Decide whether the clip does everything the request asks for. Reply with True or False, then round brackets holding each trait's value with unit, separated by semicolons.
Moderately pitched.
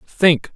True (165 Hz)